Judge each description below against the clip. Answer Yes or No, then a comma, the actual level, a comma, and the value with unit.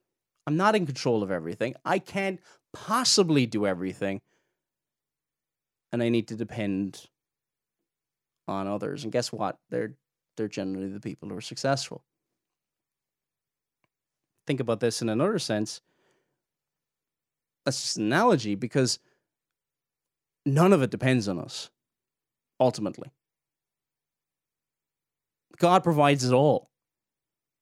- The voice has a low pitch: Yes, low, 125 Hz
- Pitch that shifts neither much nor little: No, wide, 6.7 semitones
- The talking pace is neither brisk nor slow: No, slow, 110 wpm